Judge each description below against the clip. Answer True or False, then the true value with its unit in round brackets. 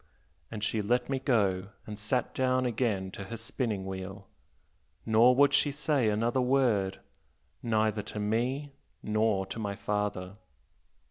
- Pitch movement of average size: True (3.8 semitones)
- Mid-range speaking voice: False (110 Hz)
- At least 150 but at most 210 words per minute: False (140 wpm)